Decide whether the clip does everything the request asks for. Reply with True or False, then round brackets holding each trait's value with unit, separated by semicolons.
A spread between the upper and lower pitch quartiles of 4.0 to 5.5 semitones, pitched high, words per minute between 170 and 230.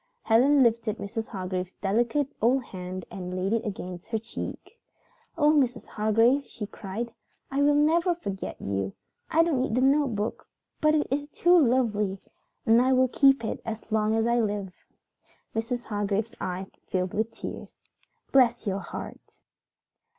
False (4.8 semitones; 225 Hz; 155 wpm)